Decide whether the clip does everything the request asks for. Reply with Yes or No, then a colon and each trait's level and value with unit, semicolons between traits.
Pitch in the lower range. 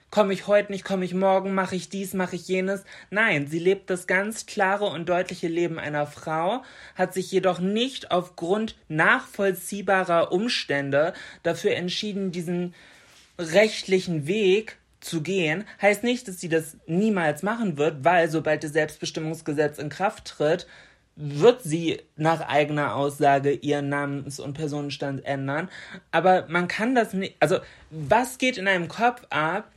No: medium, 180 Hz